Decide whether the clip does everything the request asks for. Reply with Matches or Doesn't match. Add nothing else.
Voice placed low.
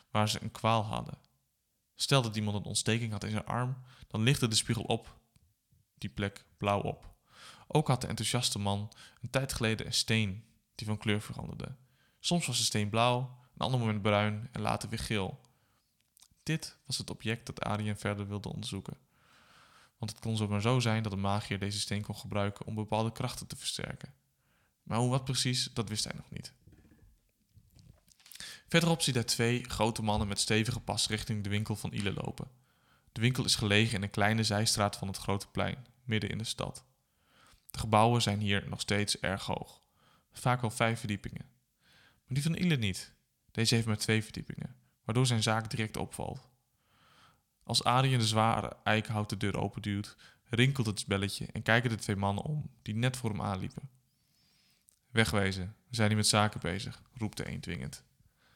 Matches